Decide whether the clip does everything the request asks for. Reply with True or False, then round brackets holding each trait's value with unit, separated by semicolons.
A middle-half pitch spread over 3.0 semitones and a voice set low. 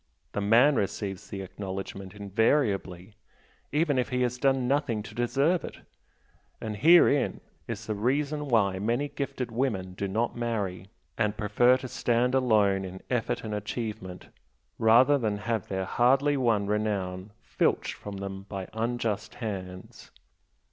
True (4.3 semitones; 110 Hz)